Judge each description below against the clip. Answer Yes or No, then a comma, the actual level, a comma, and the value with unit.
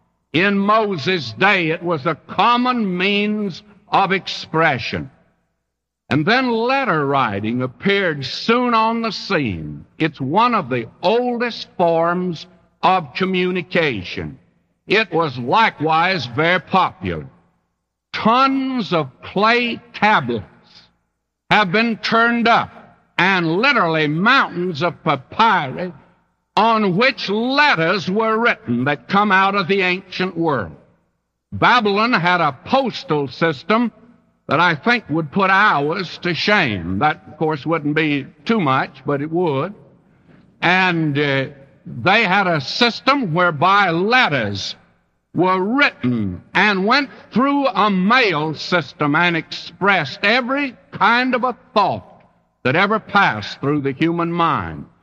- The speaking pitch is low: No, medium, 180 Hz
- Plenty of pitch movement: Yes, wide, 6.2 semitones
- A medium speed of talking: No, slow, 120 wpm